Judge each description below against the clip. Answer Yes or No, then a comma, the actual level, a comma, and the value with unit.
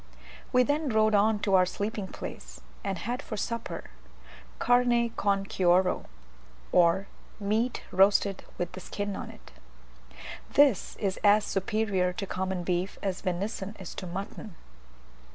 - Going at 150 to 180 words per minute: No, slow, 135 wpm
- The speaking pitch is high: Yes, high, 200 Hz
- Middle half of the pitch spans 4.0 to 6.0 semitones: No, average, 2.8 semitones